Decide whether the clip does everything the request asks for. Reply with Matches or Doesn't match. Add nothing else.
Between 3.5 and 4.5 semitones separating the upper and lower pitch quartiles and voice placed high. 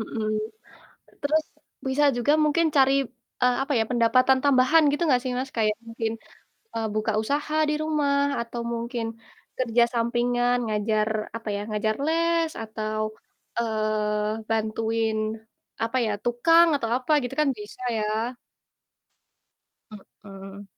Matches